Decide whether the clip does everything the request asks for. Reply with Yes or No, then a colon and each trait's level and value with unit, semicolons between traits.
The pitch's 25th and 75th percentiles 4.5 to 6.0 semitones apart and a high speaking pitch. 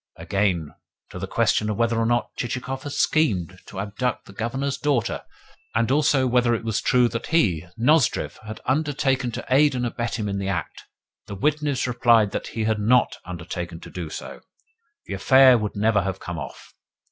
No: average, 4.8 semitones; low, 115 Hz